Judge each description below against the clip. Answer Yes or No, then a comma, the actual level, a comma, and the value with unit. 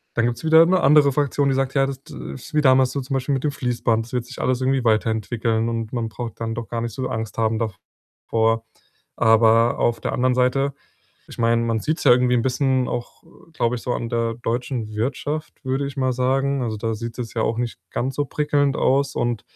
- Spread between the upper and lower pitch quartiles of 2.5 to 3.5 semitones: Yes, average, 2.9 semitones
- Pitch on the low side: Yes, low, 125 Hz